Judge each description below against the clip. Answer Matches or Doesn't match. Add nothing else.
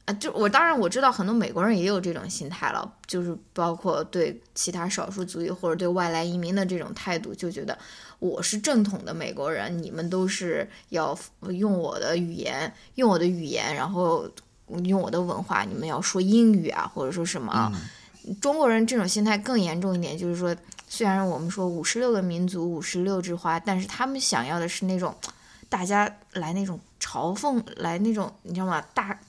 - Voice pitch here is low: Doesn't match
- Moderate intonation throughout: Matches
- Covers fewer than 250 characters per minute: Doesn't match